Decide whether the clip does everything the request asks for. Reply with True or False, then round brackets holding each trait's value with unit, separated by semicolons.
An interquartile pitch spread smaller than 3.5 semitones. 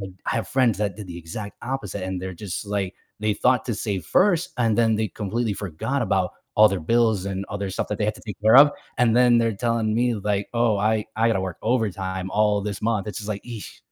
True (2.8 semitones)